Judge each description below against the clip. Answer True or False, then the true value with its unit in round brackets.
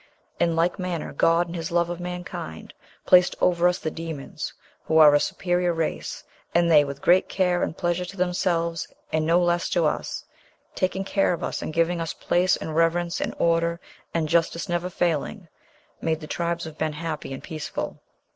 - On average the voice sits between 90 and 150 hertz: False (170 Hz)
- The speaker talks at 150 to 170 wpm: False (185 wpm)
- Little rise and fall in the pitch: True (1.6 semitones)